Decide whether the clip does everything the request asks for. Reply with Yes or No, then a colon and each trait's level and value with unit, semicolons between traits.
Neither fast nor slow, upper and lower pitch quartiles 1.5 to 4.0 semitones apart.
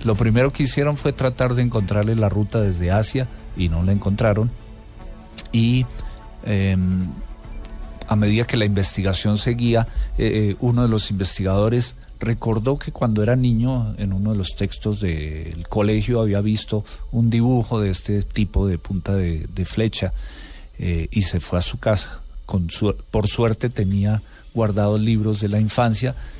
Yes: average, 160 wpm; average, 3.0 semitones